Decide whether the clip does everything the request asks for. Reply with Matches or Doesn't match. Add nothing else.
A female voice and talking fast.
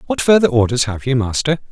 Doesn't match